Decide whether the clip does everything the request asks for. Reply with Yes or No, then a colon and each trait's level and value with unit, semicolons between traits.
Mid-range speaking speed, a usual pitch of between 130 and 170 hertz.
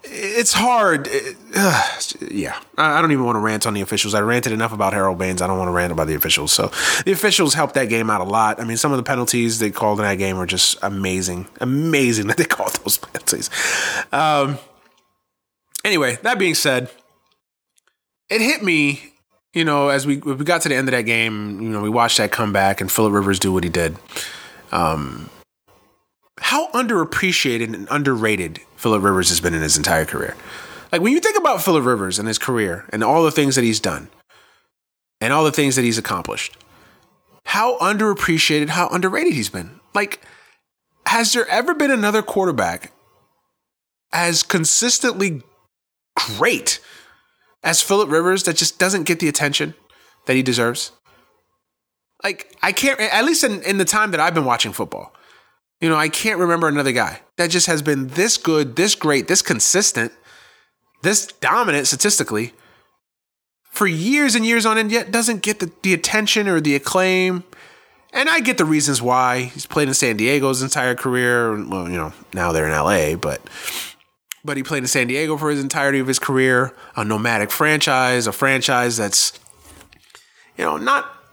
Yes: average, 180 wpm; medium, 140 Hz